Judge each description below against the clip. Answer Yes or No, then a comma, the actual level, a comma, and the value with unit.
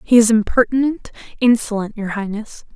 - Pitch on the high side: Yes, high, 225 Hz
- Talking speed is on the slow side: Yes, slow, 130 wpm